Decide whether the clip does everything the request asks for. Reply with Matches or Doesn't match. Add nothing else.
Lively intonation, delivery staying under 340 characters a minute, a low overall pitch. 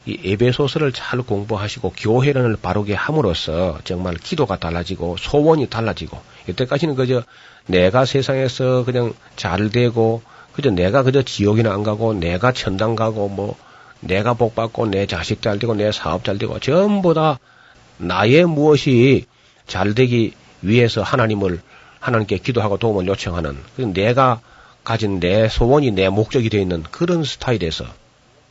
Doesn't match